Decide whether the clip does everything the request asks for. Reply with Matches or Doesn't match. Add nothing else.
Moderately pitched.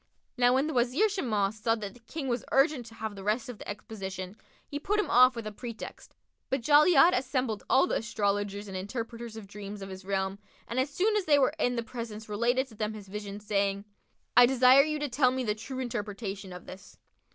Doesn't match